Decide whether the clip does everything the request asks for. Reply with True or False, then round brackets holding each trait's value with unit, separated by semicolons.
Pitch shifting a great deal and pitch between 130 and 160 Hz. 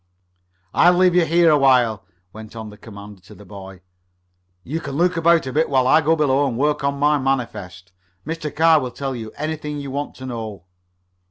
True (5.9 semitones; 135 Hz)